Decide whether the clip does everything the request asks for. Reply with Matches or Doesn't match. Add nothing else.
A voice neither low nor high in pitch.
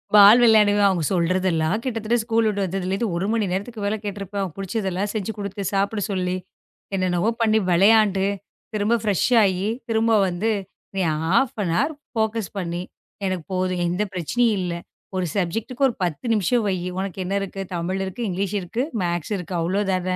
Doesn't match